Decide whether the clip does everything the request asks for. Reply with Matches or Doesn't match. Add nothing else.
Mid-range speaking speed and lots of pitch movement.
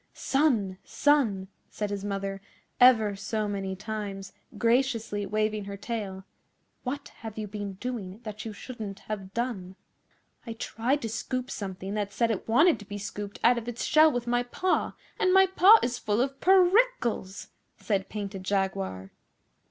Doesn't match